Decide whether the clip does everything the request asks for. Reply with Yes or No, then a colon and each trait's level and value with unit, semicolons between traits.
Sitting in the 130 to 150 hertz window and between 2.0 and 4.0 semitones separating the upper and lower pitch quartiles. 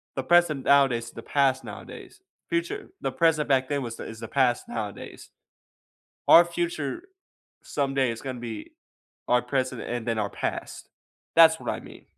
No: low, 135 Hz; average, 4.6 semitones